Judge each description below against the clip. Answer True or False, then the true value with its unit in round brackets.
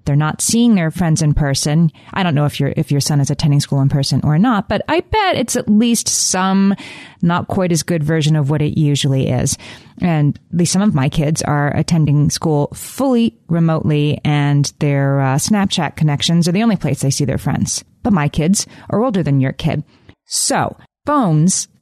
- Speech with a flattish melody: False (4.8 semitones)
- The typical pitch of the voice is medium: True (155 Hz)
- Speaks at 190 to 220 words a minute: True (200 wpm)